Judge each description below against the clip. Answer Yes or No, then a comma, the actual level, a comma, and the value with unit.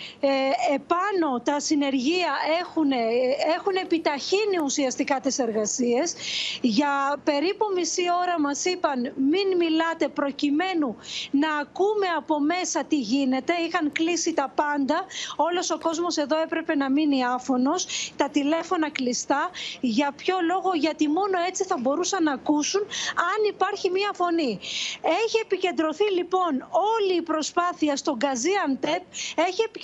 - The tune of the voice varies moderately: Yes, average, 4.0 semitones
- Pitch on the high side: Yes, very high, 320 Hz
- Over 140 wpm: No, average, 125 wpm